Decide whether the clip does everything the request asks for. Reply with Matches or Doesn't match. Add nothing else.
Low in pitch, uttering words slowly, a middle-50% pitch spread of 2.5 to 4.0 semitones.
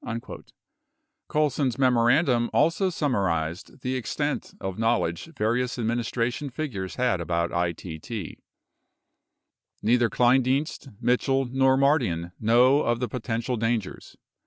Matches